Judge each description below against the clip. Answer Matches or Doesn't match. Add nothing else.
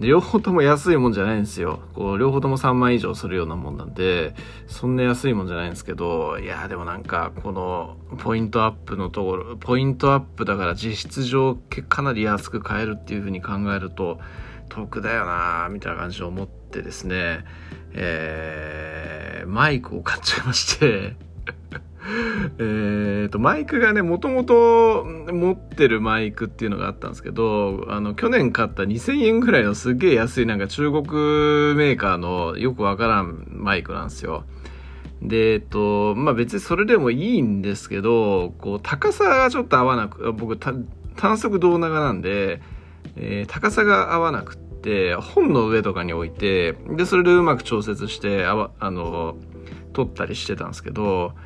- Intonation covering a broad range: Matches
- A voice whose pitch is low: Matches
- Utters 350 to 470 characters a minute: Doesn't match